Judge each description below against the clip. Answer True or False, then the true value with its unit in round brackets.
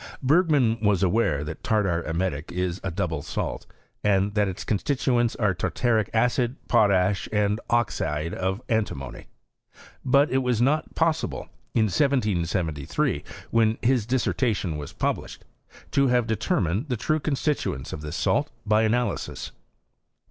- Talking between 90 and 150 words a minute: True (140 wpm)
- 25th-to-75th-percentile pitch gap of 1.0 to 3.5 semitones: False (5.2 semitones)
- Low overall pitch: True (110 Hz)